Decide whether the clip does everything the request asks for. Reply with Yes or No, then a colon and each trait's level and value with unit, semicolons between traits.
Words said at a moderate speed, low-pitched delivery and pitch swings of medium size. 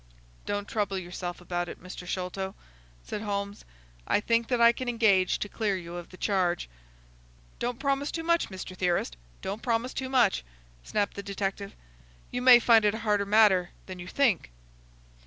No: average, 170 wpm; high, 200 Hz; average, 4.1 semitones